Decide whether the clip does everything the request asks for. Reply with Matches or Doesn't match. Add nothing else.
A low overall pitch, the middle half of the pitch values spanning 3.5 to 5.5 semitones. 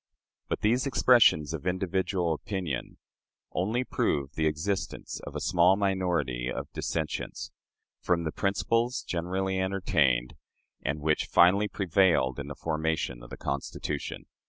Matches